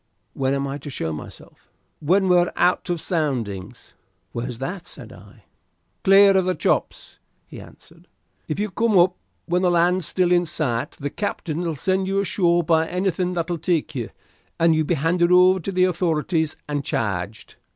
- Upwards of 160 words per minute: Yes, average, 170 wpm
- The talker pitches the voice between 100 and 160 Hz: No, medium, 170 Hz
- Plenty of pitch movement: No, average, 4.1 semitones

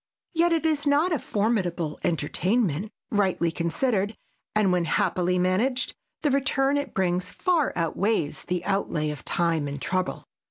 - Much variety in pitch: Yes, wide, 7.2 semitones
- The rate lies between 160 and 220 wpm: No, average, 145 wpm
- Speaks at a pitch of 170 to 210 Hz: Yes, high, 190 Hz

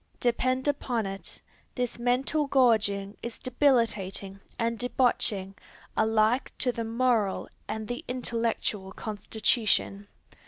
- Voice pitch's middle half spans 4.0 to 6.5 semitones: No, average, 3.1 semitones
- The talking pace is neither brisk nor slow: No, slow, 105 wpm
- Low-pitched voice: No, high, 230 Hz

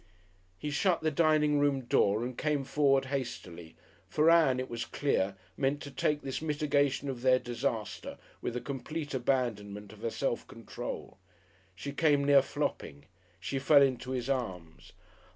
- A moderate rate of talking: Yes, average, 155 wpm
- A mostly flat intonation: No, average, 3.4 semitones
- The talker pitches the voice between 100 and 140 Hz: Yes, low, 135 Hz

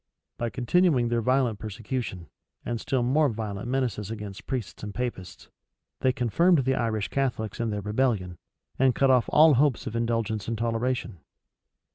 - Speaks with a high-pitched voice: No, low, 115 Hz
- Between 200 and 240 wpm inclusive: No, average, 155 wpm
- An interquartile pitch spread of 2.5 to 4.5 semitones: Yes, average, 3.3 semitones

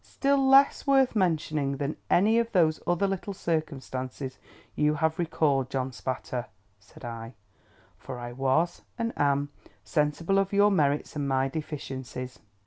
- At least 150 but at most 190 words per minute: No, average, 140 wpm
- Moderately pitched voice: Yes, medium, 150 Hz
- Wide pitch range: Yes, wide, 6.0 semitones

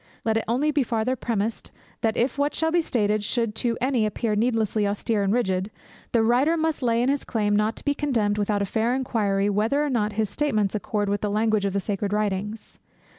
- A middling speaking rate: No, fast, 220 wpm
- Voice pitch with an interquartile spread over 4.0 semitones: No, average, 3.2 semitones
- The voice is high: Yes, high, 220 Hz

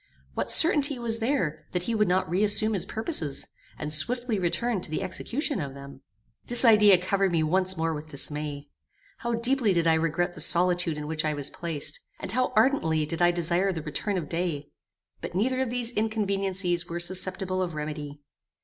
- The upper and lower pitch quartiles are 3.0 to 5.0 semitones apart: No, wide, 5.6 semitones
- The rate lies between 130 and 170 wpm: No, average, 190 wpm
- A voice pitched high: No, medium, 180 Hz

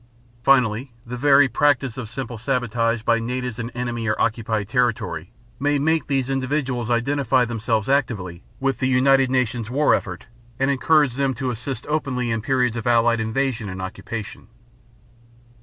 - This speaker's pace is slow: No, average, 155 wpm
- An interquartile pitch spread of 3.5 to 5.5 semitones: No, average, 2.9 semitones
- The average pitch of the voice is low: Yes, low, 125 Hz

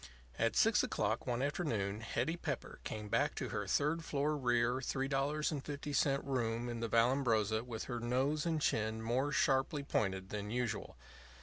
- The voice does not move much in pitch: No, average, 4.1 semitones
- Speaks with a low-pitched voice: Yes, low, 125 Hz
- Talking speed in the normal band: Yes, average, 150 wpm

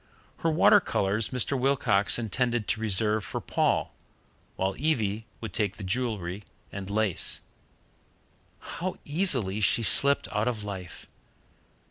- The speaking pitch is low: Yes, low, 110 Hz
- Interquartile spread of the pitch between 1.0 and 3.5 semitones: No, average, 4.2 semitones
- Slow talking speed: Yes, slow, 125 wpm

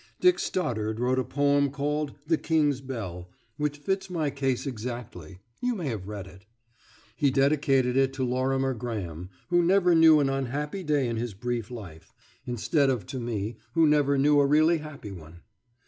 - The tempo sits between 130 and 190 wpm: Yes, average, 175 wpm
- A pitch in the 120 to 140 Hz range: Yes, low, 135 Hz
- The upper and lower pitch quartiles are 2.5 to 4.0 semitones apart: No, average, 4.4 semitones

